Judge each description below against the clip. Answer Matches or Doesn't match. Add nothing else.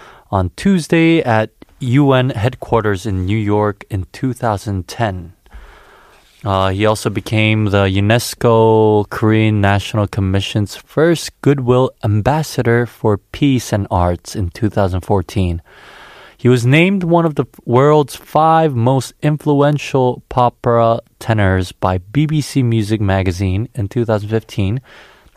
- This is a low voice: Matches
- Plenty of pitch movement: Doesn't match